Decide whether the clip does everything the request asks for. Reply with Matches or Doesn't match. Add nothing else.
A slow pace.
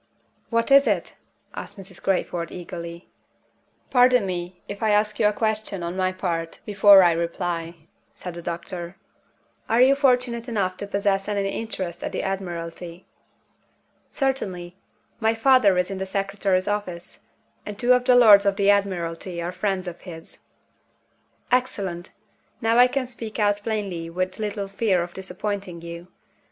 Doesn't match